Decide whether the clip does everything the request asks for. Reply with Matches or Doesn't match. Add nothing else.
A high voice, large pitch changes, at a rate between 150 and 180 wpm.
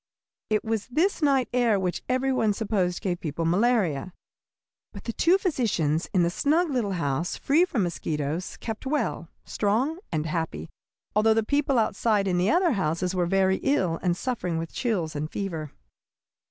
Matches